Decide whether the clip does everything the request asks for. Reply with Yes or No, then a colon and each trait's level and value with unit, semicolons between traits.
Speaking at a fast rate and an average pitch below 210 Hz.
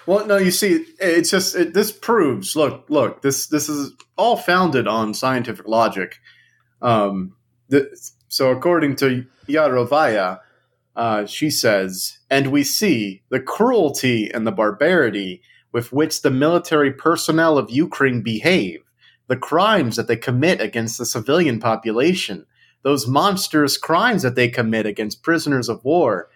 No: average, 145 wpm; low, 135 Hz